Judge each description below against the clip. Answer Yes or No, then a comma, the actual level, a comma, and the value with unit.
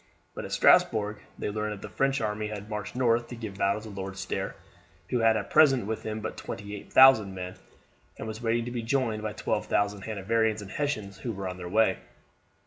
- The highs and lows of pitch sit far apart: No, narrow, 2.4 semitones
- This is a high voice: No, low, 110 Hz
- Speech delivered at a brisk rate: Yes, fast, 220 wpm